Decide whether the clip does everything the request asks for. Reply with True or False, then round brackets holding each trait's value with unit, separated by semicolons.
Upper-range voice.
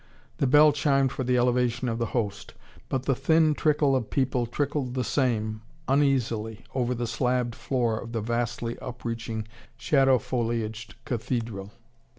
False (125 Hz)